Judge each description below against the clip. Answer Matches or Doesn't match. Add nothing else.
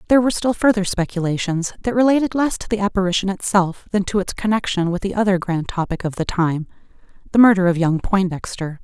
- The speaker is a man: Doesn't match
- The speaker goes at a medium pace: Matches